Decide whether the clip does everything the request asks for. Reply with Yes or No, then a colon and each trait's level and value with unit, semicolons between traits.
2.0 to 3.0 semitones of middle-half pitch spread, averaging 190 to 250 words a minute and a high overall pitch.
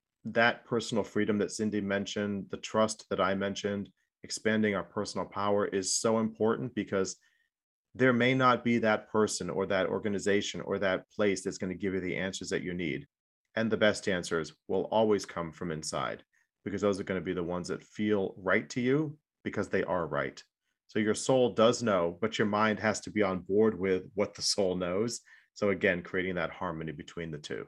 No: average, 2.7 semitones; average, 200 wpm; low, 100 Hz